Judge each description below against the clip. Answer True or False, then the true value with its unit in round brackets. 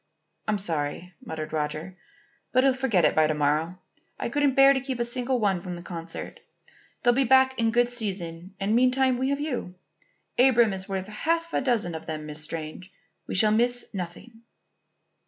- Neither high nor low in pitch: False (210 Hz)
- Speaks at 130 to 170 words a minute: False (185 wpm)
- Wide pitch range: True (7.0 semitones)